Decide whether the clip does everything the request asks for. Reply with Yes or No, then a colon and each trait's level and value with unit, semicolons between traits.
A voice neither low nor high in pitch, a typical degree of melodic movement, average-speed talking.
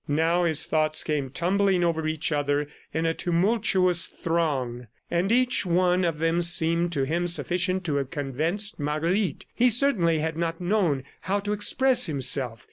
Yes: medium, 170 Hz; average, 3.3 semitones; average, 160 wpm